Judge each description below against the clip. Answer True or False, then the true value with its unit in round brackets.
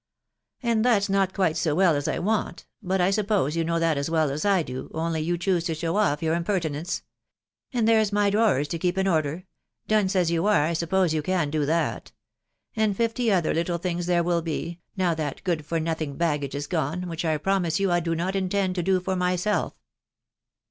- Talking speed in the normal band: False (225 wpm)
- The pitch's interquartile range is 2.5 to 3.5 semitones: True (3.2 semitones)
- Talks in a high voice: False (175 Hz)